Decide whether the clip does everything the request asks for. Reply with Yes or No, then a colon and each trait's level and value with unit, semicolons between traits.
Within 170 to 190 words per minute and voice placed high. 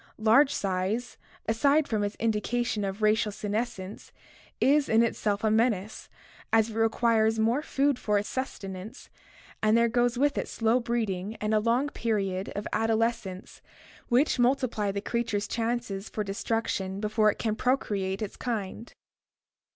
No: average, 150 wpm; high, 220 Hz